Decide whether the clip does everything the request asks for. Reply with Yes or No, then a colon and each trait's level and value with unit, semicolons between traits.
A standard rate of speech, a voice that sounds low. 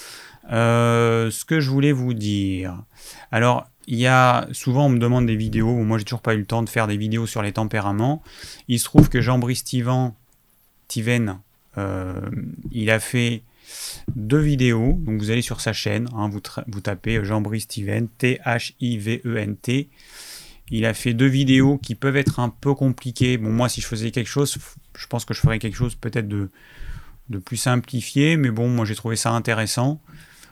Yes: average, 190 wpm; low, 120 Hz